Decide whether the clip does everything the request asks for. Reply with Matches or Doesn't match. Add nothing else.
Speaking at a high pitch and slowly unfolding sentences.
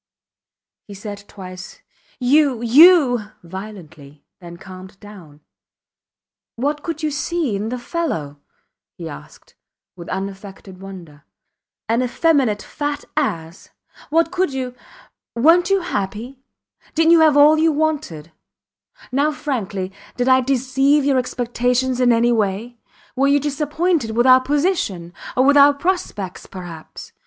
Matches